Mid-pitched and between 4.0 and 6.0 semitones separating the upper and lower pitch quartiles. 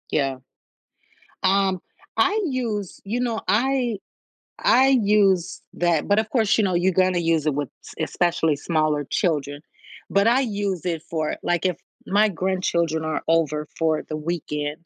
Yes: medium, 180 Hz; average, 4.7 semitones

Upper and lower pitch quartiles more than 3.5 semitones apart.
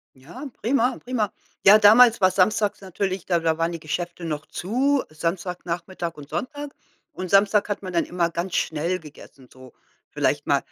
Yes: average, 4.1 semitones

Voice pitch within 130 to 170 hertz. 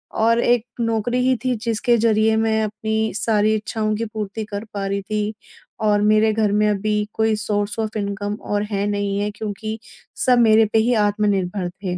No: high, 215 Hz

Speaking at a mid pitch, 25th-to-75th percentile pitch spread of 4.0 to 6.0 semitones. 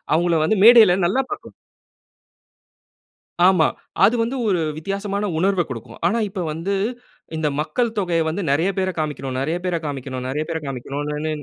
Yes: medium, 170 Hz; average, 4.8 semitones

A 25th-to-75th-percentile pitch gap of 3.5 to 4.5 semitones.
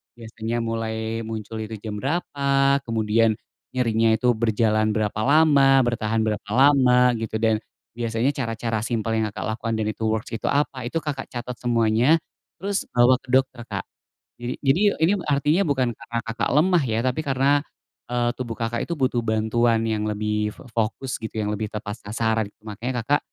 No: average, 3.1 semitones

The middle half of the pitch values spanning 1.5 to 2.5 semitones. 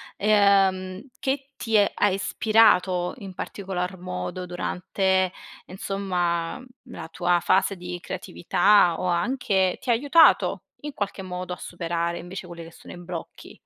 Yes: narrow, 2.2 semitones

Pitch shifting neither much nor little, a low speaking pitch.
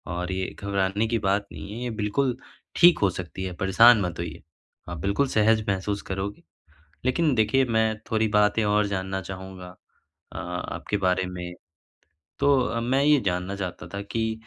Yes: average, 3.1 semitones; low, 100 Hz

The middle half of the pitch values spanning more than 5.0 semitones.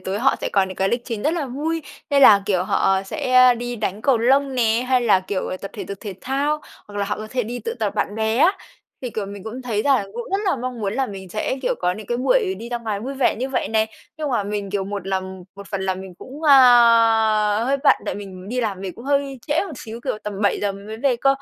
No: average, 4.6 semitones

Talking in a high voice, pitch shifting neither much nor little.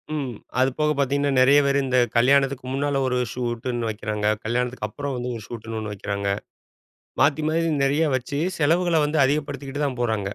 No: low, 130 Hz; average, 3.3 semitones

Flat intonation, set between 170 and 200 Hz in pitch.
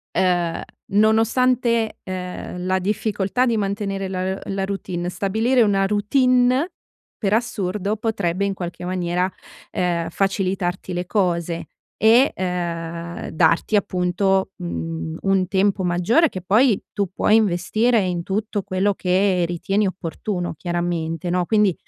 No: average, 3.0 semitones; high, 190 Hz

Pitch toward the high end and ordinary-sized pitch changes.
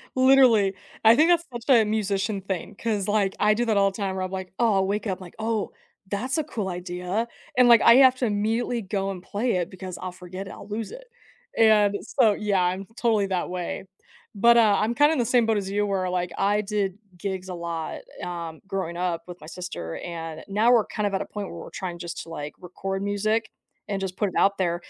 Yes: high, 200 Hz; average, 3.2 semitones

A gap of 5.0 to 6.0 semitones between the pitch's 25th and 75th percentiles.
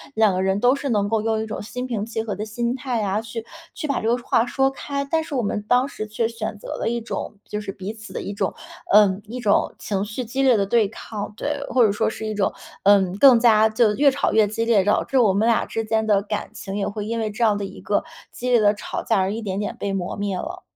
No: average, 2.7 semitones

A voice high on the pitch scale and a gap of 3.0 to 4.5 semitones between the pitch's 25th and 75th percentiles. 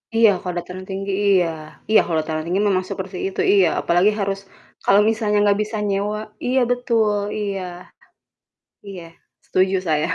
No: high, 195 Hz; narrow, 2.4 semitones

